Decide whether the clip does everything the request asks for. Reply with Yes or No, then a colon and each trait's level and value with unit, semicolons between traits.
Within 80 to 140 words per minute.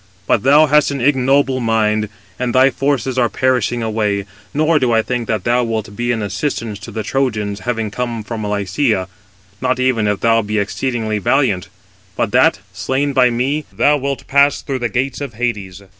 No: average, 185 wpm